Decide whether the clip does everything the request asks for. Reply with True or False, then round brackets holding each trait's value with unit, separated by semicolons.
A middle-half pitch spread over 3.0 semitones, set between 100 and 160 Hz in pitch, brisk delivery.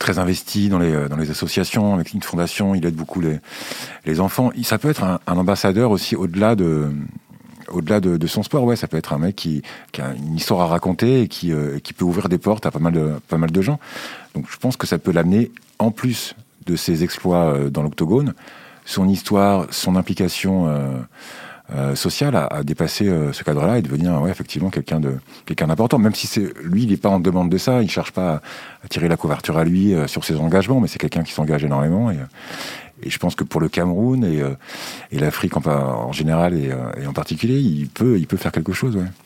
False (4.3 semitones; 90 Hz; 230 wpm)